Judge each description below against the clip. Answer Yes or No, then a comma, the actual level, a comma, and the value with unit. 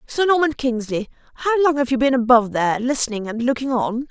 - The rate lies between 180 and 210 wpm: Yes, fast, 205 wpm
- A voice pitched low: No, very high, 250 Hz